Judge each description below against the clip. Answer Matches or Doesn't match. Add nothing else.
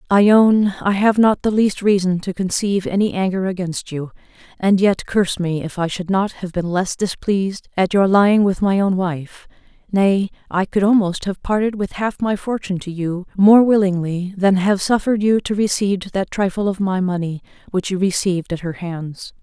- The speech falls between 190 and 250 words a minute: Matches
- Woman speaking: Matches